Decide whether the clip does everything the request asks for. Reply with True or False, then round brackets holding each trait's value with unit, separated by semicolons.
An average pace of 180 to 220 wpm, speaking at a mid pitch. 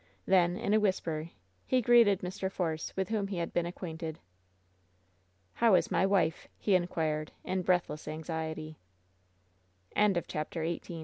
False (135 wpm; 175 Hz)